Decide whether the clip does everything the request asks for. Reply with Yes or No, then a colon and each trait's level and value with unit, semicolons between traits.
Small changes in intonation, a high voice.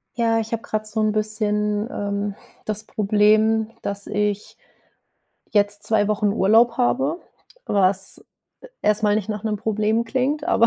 Yes: narrow, 1.3 semitones; high, 215 Hz